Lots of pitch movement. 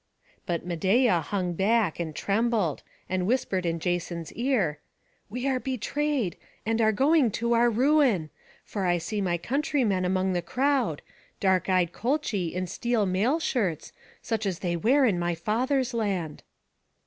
Yes: wide, 5.8 semitones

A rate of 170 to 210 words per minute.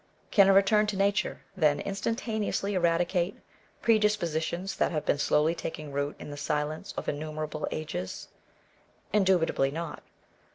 No: average, 140 wpm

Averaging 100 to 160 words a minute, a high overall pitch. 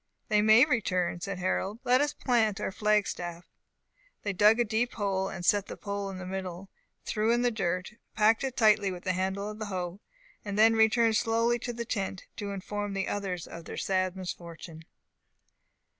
No: average, 190 wpm; high, 205 Hz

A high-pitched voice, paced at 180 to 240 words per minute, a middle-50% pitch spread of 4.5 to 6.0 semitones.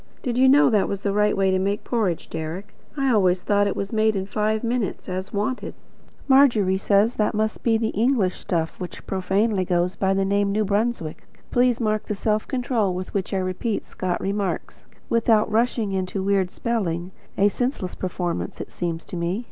No: high, 200 Hz; average, 190 wpm; average, 3.0 semitones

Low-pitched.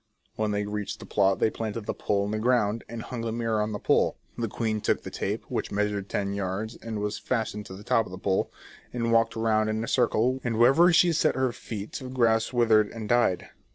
Yes: low, 110 Hz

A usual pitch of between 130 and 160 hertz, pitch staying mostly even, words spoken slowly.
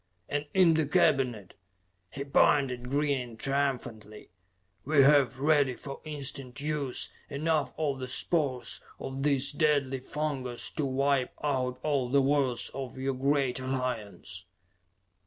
Yes: low, 135 Hz; narrow, 2.3 semitones; slow, 125 wpm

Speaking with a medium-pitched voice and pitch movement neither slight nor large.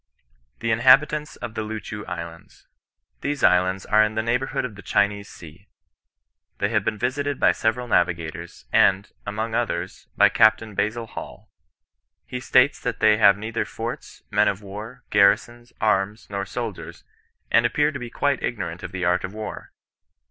No: low, 110 Hz; average, 3.3 semitones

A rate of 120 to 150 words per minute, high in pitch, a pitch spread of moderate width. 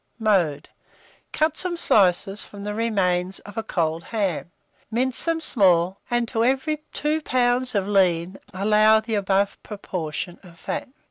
Yes: average, 145 wpm; high, 205 Hz; average, 4.7 semitones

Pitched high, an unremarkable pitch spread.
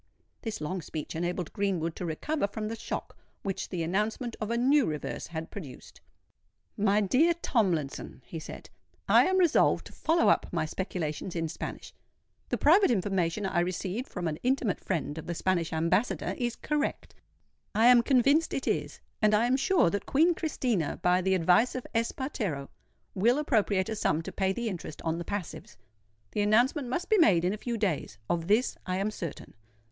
No: high, 200 Hz; wide, 6.2 semitones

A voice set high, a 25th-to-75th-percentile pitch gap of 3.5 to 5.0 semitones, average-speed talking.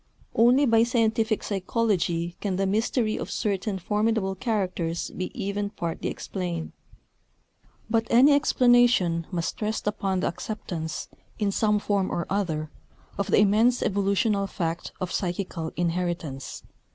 No: high, 200 Hz; average, 4.0 semitones; slow, 130 wpm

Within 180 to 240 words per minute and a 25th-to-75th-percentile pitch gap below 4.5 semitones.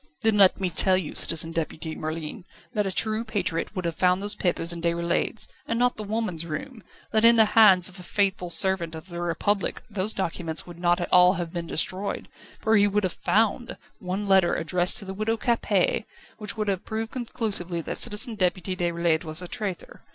Yes: average, 200 wpm; average, 3.7 semitones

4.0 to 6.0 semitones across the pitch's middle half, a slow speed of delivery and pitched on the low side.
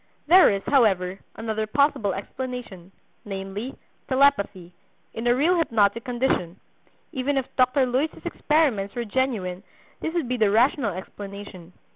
No: average, 5.1 semitones; slow, 130 wpm; high, 230 Hz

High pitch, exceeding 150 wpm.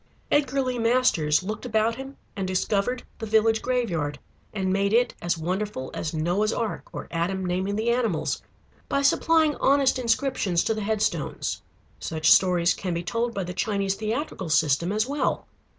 Yes: high, 210 Hz; average, 165 wpm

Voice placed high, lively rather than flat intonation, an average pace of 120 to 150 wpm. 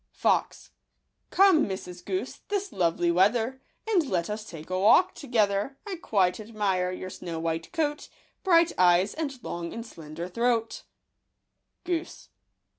Yes: high, 210 Hz; wide, 8.5 semitones; average, 145 wpm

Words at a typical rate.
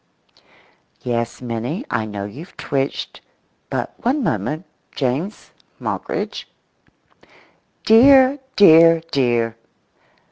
No: slow, 70 wpm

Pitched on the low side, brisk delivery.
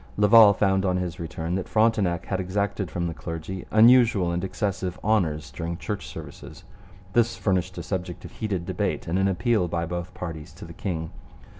No: very low, 90 Hz; average, 180 wpm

